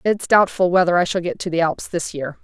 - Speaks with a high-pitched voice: No, medium, 175 Hz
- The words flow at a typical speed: No, fast, 270 wpm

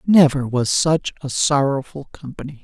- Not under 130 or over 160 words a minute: Yes, slow, 135 wpm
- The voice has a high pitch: No, medium, 140 Hz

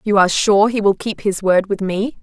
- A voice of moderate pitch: No, high, 205 Hz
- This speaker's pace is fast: Yes, fast, 270 wpm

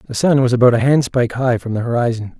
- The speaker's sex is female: No, male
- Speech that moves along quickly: Yes, fast, 250 wpm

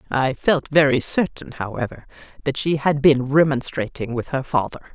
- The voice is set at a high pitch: No, medium, 140 Hz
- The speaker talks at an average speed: Yes, average, 160 wpm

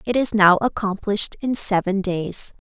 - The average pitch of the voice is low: No, high, 205 Hz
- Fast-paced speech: No, average, 155 wpm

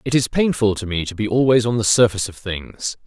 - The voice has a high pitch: No, low, 110 Hz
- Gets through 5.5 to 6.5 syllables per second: Yes, 5.9 syllables/s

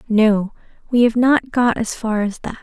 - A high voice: Yes, high, 225 Hz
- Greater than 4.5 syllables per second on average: No, 4.4 syllables/s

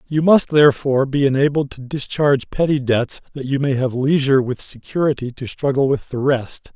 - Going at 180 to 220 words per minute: Yes, average, 185 wpm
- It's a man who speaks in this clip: Yes, male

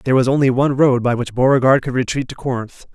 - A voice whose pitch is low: Yes, low, 130 Hz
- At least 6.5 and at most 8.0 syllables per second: Yes, 6.9 syllables/s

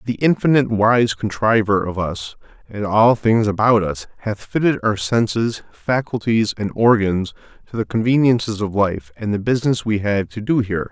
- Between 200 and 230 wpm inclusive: No, average, 170 wpm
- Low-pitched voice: Yes, low, 110 Hz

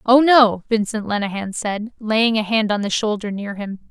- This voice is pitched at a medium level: No, high, 215 Hz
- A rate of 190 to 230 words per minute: Yes, average, 200 wpm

